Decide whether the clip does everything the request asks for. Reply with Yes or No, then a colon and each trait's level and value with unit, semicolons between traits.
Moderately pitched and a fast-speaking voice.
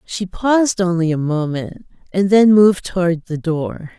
No: medium, 180 Hz; average, 165 wpm